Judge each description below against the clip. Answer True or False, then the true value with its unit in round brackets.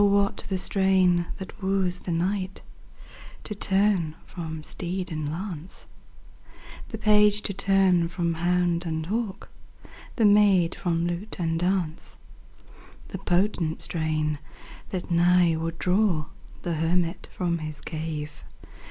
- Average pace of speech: False (125 wpm)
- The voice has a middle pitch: True (180 Hz)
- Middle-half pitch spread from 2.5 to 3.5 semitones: True (2.8 semitones)